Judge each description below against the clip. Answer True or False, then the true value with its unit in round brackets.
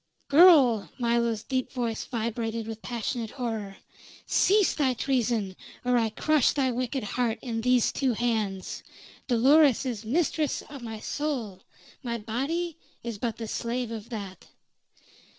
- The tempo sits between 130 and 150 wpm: True (135 wpm)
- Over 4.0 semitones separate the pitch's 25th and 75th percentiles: False (3.0 semitones)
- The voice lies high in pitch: True (235 Hz)